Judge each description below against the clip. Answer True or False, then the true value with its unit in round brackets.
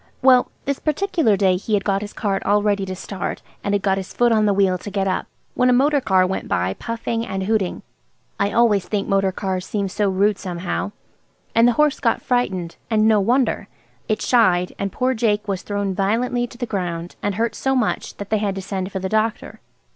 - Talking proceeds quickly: True (220 wpm)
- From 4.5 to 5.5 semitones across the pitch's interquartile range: False (3.2 semitones)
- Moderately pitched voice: False (205 Hz)